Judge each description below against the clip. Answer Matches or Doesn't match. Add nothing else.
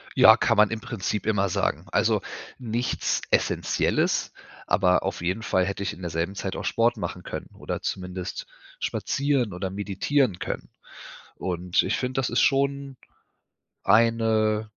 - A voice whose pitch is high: Doesn't match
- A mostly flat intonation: Doesn't match